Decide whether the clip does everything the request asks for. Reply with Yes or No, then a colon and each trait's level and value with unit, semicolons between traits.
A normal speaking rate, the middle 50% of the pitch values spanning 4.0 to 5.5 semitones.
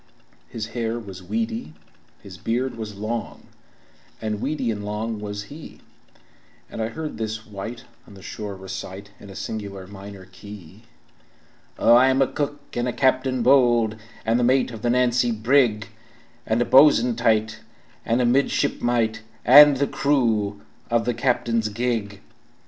No: average, 155 wpm; average, 2.9 semitones